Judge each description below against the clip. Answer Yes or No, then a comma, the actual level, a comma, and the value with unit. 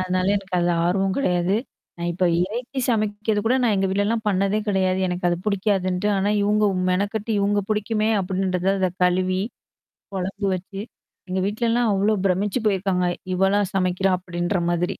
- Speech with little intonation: Yes, narrow, 2.2 semitones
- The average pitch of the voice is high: Yes, high, 195 Hz